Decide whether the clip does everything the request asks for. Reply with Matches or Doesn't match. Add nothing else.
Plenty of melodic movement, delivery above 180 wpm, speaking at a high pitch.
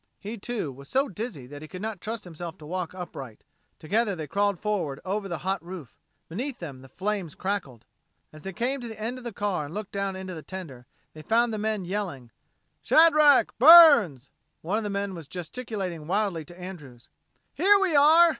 Matches